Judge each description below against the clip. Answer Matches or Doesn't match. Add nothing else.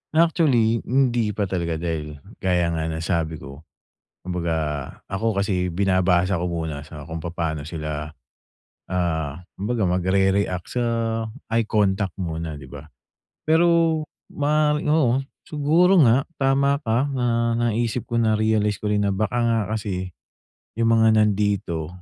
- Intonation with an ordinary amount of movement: Doesn't match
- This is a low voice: Matches